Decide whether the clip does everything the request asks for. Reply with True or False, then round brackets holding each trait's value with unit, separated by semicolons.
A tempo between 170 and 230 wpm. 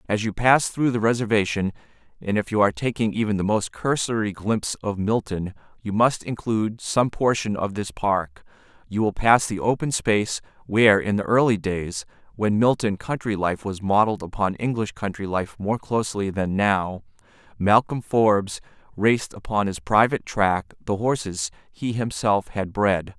False (160 wpm)